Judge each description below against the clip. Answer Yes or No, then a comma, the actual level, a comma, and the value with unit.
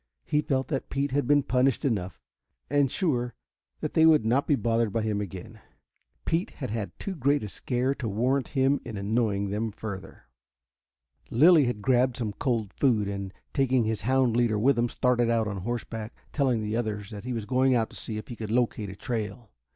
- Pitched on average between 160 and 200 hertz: No, low, 120 Hz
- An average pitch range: Yes, average, 3.7 semitones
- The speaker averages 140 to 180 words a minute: No, fast, 205 wpm